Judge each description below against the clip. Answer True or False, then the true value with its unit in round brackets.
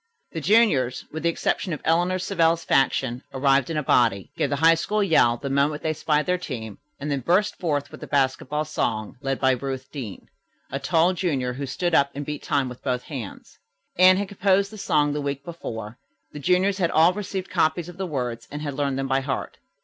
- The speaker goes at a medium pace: False (215 wpm)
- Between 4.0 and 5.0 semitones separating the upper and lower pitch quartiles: True (4.6 semitones)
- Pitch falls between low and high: True (145 Hz)